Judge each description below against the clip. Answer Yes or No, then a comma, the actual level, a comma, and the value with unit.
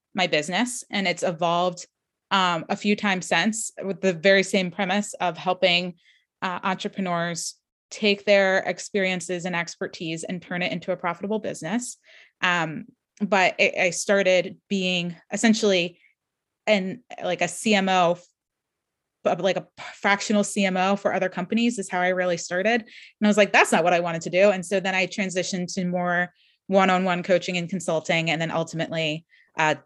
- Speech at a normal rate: Yes, average, 165 wpm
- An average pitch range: No, narrow, 2.2 semitones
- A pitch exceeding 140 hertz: Yes, medium, 185 Hz